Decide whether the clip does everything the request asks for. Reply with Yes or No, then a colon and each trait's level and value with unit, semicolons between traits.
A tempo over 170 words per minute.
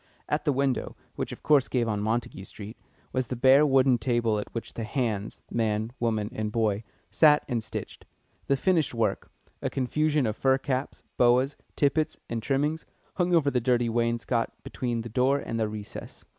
Yes: average, 180 wpm